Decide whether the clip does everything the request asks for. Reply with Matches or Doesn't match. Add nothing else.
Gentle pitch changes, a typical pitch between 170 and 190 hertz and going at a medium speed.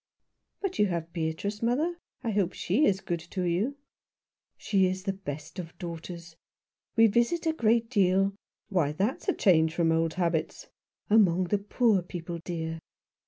Doesn't match